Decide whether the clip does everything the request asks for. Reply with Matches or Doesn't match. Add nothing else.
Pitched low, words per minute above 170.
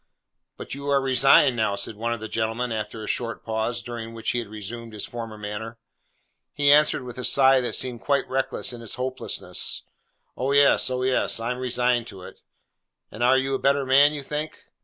Matches